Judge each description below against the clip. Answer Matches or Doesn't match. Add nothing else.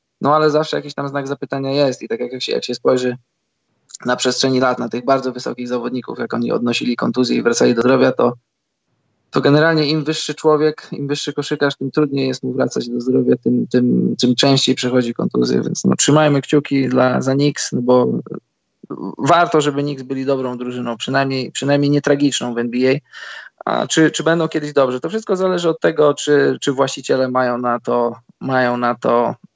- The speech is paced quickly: Matches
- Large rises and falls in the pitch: Doesn't match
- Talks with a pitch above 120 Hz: Matches